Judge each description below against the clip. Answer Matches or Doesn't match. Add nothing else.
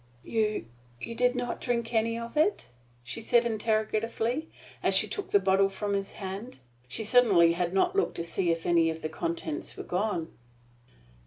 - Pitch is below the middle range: Doesn't match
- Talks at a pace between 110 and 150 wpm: Doesn't match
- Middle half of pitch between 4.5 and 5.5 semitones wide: Matches